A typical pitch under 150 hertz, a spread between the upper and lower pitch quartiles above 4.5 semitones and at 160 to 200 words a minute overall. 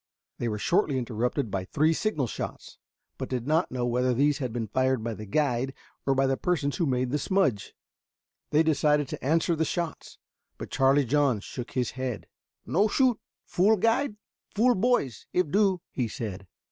Yes: low, 135 Hz; average, 5.3 semitones; average, 185 wpm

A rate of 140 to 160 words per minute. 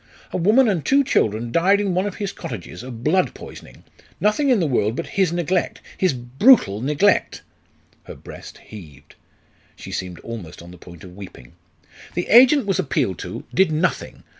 No: average, 175 wpm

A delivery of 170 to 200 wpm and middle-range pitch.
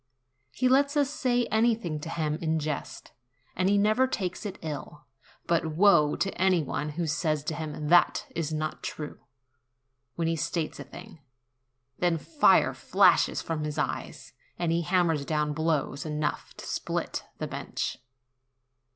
No: average, 155 wpm; medium, 165 Hz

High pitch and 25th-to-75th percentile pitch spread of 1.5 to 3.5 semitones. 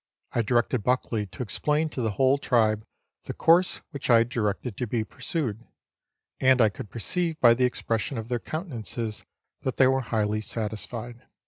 No: low, 120 Hz; average, 3.2 semitones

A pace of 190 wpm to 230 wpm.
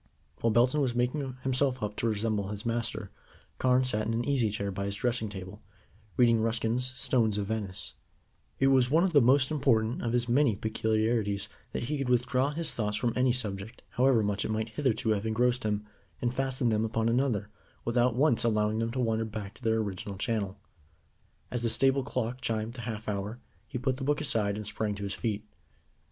Yes: average, 200 wpm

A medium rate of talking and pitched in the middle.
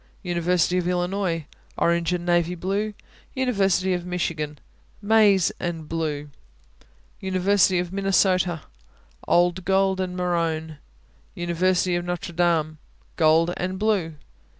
No: slow, 110 wpm; medium, 175 Hz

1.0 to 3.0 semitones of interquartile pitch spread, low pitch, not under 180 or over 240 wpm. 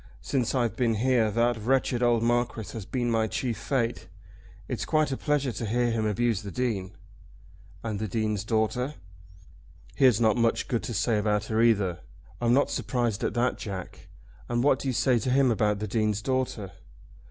Yes: narrow, 2.6 semitones; low, 115 Hz; average, 185 wpm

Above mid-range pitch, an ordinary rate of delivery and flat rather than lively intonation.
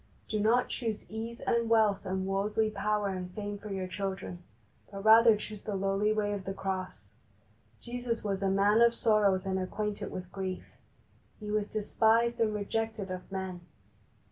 Yes: high, 205 Hz; average, 170 wpm; narrow, 2.2 semitones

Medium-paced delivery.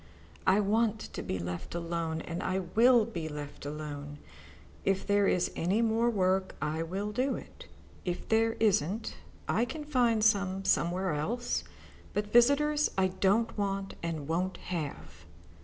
Yes: average, 150 wpm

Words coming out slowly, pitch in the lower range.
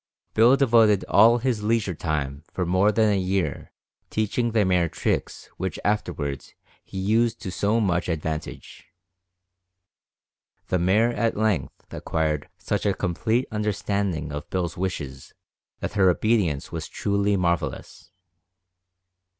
Yes: slow, 125 wpm; very low, 95 Hz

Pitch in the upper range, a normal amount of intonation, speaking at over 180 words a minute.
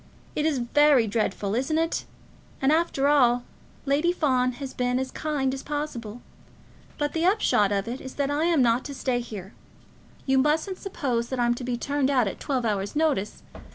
Yes: very high, 265 Hz; average, 3.7 semitones; average, 190 wpm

